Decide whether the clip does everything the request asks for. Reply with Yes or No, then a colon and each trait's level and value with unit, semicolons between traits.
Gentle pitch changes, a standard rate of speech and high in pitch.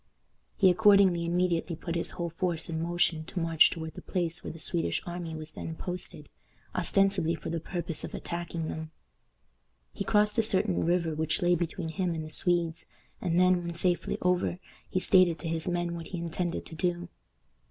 No: narrow, 1.7 semitones; average, 185 wpm; medium, 170 Hz